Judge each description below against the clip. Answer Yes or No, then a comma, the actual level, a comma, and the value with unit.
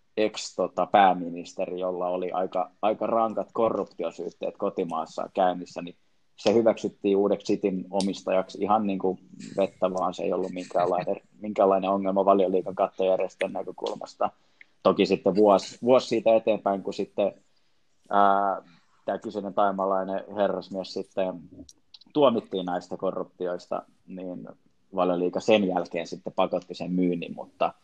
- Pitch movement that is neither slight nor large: No, narrow, 1.7 semitones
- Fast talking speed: No, average, 120 wpm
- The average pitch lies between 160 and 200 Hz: No, very low, 95 Hz